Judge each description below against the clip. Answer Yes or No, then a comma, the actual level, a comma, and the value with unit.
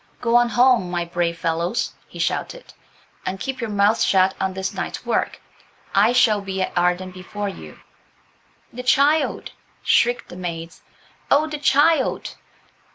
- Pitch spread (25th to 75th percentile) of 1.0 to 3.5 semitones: No, wide, 5.6 semitones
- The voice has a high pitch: Yes, high, 200 Hz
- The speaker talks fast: No, average, 150 wpm